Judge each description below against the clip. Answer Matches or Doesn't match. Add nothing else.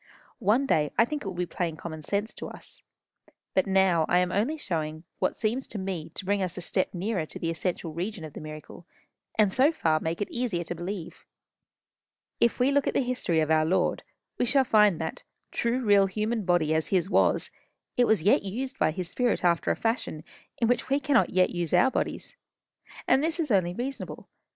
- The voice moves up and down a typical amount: Doesn't match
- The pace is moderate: Doesn't match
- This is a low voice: Doesn't match